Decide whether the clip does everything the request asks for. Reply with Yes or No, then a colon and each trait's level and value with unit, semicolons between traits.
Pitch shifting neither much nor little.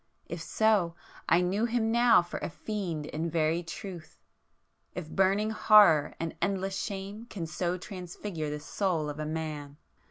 Yes: average, 4.1 semitones